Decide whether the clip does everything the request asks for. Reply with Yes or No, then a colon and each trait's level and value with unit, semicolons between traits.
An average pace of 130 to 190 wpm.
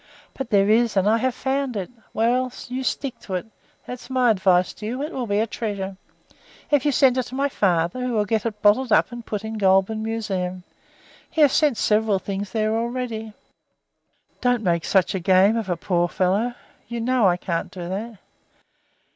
No: fast, 205 wpm